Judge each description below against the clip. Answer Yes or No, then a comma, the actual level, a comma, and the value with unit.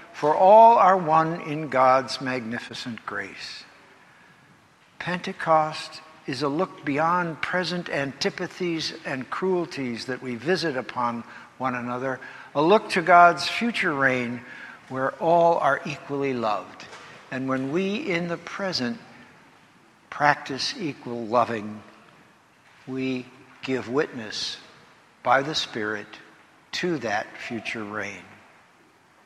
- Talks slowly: Yes, slow, 110 wpm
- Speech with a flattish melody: No, average, 5.2 semitones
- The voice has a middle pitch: Yes, medium, 145 Hz